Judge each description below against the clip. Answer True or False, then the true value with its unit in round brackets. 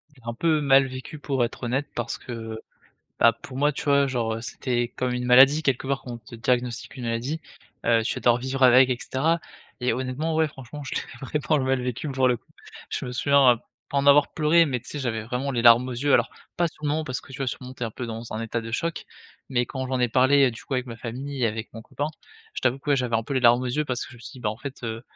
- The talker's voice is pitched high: False (130 Hz)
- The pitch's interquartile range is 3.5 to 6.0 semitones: False (2.7 semitones)